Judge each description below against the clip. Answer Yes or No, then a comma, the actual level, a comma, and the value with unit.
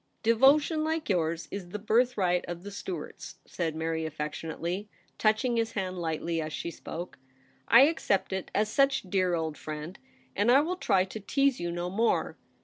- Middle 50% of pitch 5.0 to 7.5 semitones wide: Yes, wide, 5.5 semitones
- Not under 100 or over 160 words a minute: No, average, 180 wpm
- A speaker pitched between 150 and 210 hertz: Yes, high, 190 Hz